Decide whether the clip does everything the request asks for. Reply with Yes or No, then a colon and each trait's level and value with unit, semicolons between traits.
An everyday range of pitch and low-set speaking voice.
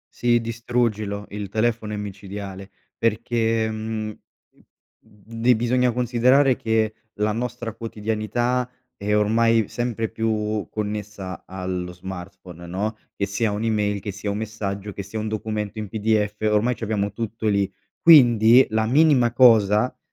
No: narrow, 2.1 semitones; low, 110 Hz